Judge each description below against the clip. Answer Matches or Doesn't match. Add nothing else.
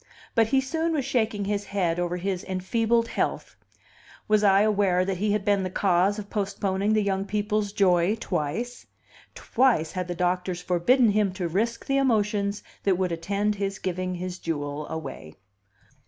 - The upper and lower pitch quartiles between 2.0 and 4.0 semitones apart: Matches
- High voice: Matches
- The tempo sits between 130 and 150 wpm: Doesn't match